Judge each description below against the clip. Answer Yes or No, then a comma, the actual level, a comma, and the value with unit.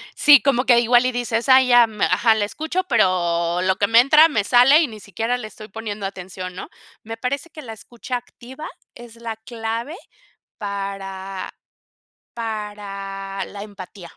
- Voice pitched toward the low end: No, high, 225 Hz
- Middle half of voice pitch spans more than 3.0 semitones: Yes, average, 3.8 semitones